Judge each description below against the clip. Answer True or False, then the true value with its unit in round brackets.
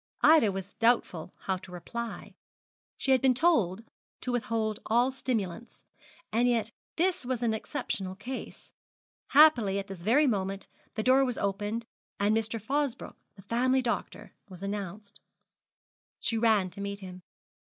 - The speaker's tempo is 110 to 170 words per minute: True (145 wpm)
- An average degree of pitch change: True (4.0 semitones)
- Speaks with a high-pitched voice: True (225 Hz)